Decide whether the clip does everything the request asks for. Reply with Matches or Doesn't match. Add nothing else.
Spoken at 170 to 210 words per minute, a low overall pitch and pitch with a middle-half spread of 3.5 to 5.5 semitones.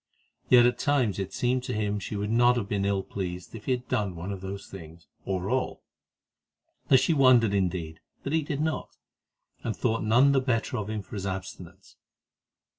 Matches